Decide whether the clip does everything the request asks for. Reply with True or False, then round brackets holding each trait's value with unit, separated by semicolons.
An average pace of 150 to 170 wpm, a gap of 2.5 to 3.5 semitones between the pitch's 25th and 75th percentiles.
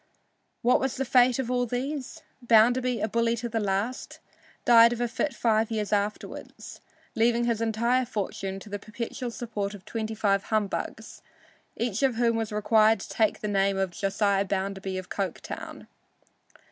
True (165 wpm; 3.0 semitones)